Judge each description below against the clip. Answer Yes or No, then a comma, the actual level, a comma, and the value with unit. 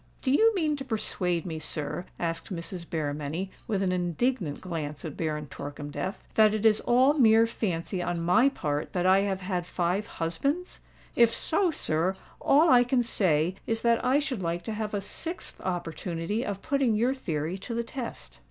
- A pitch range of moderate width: No, wide, 6.2 semitones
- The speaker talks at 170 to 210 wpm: Yes, average, 180 wpm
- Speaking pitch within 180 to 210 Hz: Yes, high, 190 Hz